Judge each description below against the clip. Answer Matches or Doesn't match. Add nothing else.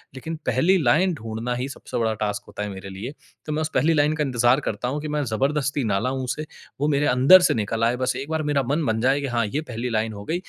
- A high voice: Doesn't match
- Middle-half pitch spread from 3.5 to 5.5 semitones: Matches